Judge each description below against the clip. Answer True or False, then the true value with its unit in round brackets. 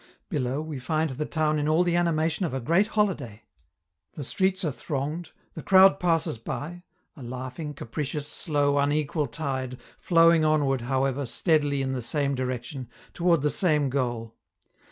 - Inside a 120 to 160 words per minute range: True (155 wpm)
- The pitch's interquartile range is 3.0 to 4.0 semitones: True (3.7 semitones)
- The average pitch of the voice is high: False (145 Hz)